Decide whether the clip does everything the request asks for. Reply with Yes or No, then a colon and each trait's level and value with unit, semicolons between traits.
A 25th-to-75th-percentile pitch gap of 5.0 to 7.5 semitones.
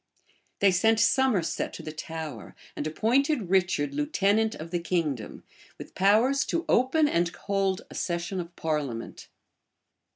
Yes: wide, 5.6 semitones